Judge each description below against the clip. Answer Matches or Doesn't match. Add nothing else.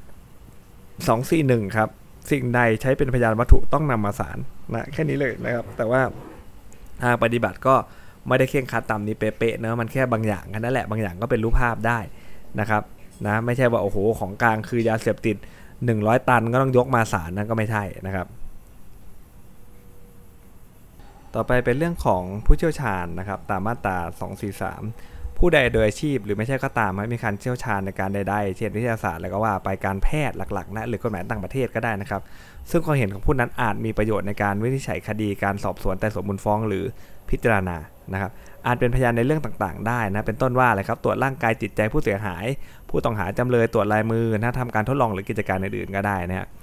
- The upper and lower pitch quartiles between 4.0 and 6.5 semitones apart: Doesn't match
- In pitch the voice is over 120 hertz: Doesn't match